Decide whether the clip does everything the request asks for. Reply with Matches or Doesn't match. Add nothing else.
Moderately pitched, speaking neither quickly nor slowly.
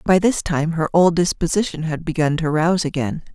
Matches